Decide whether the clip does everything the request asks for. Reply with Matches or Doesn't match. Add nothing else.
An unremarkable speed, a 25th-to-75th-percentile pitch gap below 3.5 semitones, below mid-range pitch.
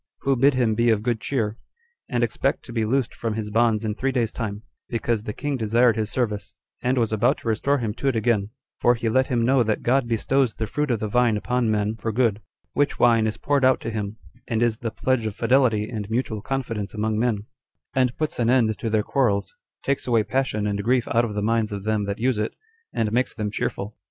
Doesn't match